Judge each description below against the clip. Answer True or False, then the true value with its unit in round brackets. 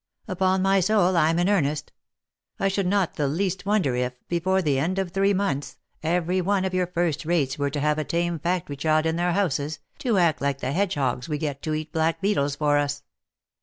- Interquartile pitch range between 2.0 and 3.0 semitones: False (4.4 semitones)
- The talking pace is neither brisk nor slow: False (210 wpm)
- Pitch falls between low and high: True (170 Hz)